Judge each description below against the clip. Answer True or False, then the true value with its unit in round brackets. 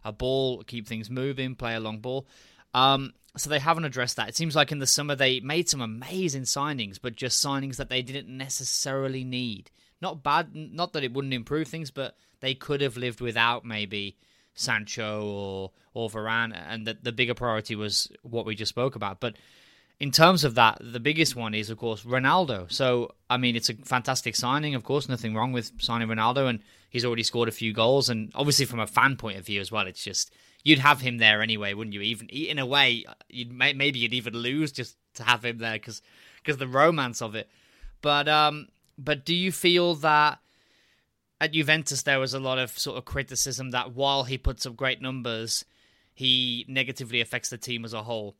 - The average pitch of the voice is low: True (125 Hz)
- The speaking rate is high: True (210 wpm)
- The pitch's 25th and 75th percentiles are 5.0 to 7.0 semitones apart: False (3.3 semitones)